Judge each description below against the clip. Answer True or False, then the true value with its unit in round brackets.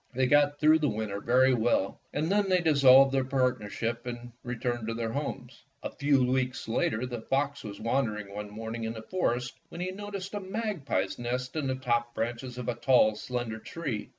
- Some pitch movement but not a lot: True (3.8 semitones)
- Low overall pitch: True (125 Hz)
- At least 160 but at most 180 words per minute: False (195 wpm)